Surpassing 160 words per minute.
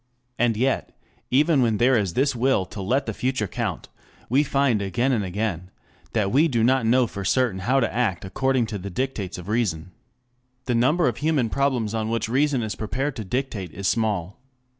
Yes: average, 195 wpm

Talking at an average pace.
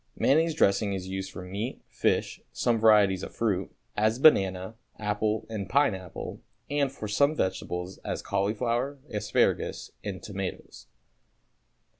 No: slow, 125 wpm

